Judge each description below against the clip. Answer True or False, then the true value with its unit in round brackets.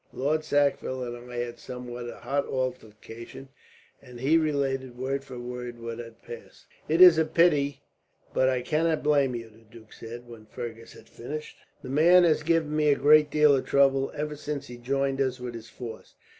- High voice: False (135 Hz)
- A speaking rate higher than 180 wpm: True (190 wpm)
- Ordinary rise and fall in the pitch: True (3.7 semitones)